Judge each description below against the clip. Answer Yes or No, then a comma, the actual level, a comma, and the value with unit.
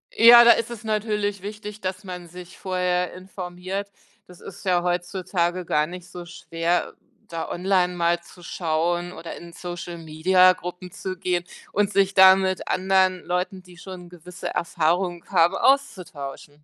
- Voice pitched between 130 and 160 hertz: No, medium, 180 Hz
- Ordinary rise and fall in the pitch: No, narrow, 1.6 semitones